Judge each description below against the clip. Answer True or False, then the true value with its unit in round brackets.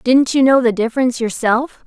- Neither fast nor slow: True (195 wpm)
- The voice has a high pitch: True (250 Hz)